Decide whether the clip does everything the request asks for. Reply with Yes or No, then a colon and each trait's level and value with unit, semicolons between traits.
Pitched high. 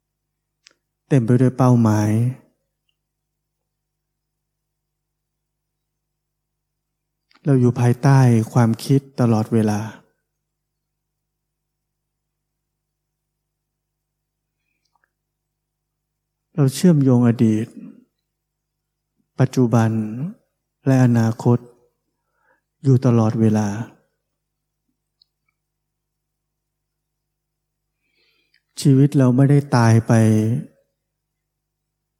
No: medium, 150 Hz